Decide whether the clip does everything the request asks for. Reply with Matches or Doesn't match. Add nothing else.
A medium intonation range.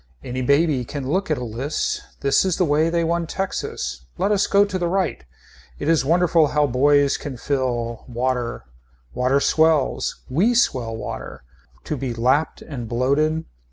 Matches